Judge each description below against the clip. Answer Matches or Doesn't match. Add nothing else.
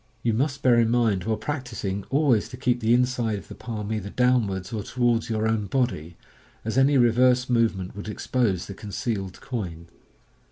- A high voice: Doesn't match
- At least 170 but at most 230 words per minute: Matches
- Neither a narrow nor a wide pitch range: Matches